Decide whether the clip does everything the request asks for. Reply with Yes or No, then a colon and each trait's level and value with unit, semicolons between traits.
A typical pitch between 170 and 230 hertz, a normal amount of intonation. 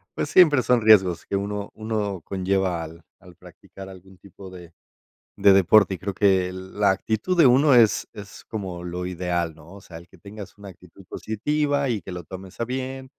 No: very low, 95 Hz; average, 3.3 semitones